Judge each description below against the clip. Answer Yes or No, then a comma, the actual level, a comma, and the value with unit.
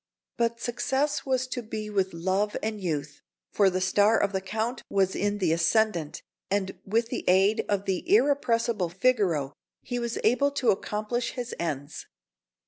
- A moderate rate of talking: Yes, average, 160 wpm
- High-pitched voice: Yes, high, 210 Hz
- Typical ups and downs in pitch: Yes, average, 4.0 semitones